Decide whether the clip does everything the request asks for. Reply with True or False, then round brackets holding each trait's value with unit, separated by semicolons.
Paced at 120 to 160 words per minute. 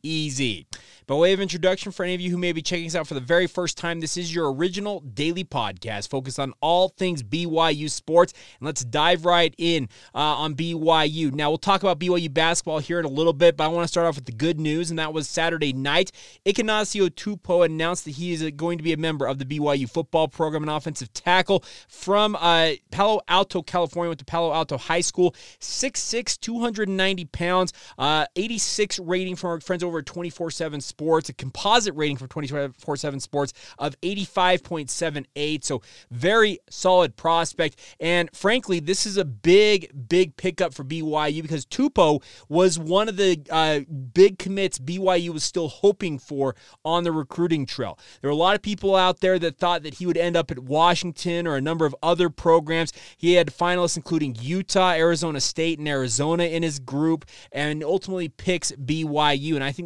False (190 wpm)